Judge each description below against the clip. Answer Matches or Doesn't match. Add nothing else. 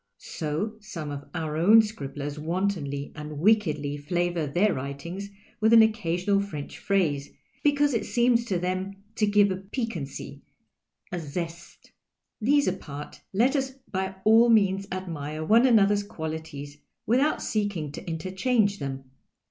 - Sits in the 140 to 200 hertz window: Matches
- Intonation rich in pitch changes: Matches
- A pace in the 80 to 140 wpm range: Matches